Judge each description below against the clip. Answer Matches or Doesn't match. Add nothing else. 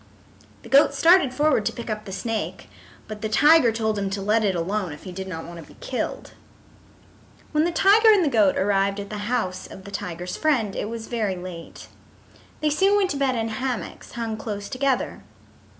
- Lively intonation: Matches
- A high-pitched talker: Matches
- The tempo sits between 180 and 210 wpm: Matches